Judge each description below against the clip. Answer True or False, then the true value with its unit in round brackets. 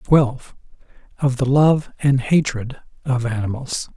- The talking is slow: True (120 wpm)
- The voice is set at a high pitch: False (130 Hz)